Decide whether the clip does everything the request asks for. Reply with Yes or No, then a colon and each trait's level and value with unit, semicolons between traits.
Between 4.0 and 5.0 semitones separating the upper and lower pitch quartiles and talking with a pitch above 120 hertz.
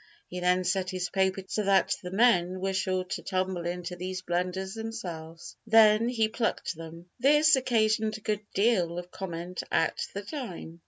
No: average, 3.4 semitones; high, 190 Hz